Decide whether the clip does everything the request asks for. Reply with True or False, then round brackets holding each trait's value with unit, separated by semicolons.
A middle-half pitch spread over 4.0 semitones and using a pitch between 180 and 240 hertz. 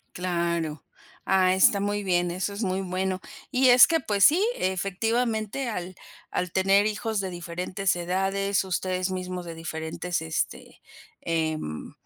False (2.4 semitones; 185 Hz)